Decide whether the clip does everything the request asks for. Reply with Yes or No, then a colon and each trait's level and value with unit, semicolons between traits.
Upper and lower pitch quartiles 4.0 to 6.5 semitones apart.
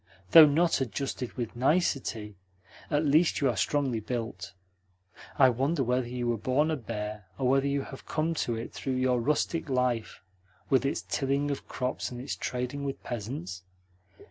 No: average, 3.1 semitones